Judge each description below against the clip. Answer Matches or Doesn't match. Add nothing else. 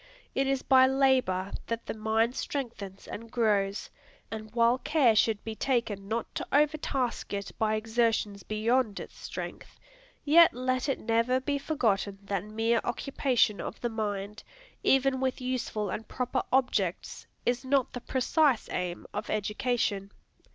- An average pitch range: Matches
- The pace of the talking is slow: Doesn't match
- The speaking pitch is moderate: Doesn't match